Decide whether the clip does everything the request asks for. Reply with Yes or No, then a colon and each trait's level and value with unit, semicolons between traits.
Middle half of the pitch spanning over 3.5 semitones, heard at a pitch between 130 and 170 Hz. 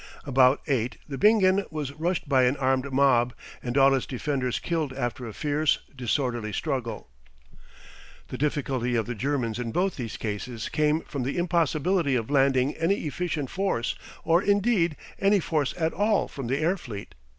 Yes: average, 4.7 semitones; medium, 140 Hz